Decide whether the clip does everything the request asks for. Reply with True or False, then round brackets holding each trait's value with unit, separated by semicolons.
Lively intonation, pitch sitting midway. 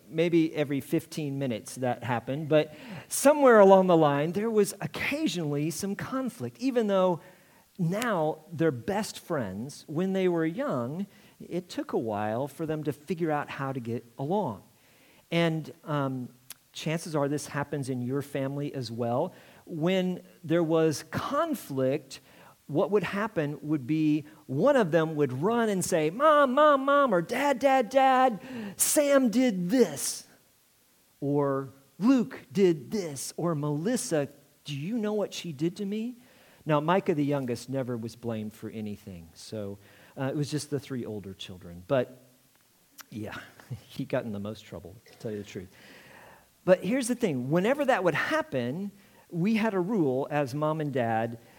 True (6.9 semitones; 155 Hz)